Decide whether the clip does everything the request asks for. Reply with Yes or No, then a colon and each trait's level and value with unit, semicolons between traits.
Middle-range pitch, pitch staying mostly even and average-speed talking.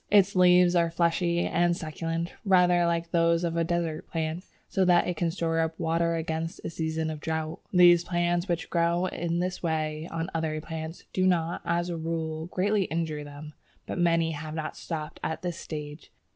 Yes: medium, 170 Hz; narrow, 1.4 semitones; average, 185 wpm